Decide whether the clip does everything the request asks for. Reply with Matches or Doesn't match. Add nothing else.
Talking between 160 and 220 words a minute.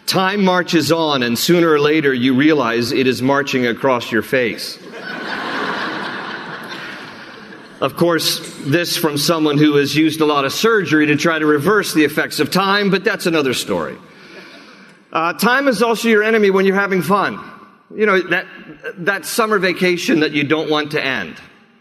Matches